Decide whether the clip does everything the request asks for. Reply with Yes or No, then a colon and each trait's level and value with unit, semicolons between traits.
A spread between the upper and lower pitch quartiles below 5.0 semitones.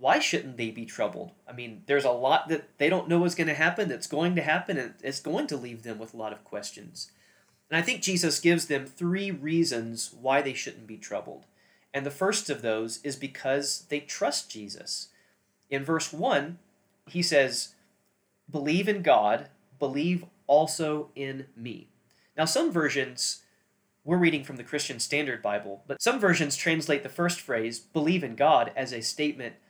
Yes: average, 4.3 semitones